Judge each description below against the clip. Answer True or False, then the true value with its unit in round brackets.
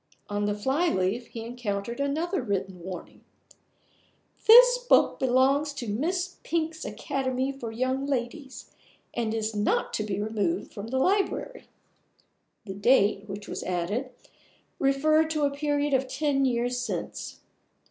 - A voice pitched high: True (260 Hz)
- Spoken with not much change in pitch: False (5.4 semitones)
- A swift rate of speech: False (135 wpm)